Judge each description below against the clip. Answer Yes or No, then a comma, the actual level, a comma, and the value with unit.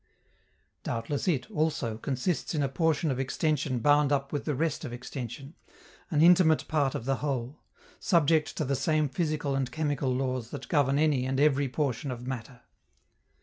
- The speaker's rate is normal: Yes, average, 170 wpm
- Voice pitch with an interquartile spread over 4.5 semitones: No, average, 2.9 semitones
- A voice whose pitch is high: No, medium, 140 Hz